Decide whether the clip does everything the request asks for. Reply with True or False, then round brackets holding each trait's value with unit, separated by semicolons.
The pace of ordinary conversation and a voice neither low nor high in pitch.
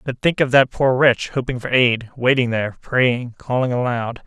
False (195 wpm; 125 Hz)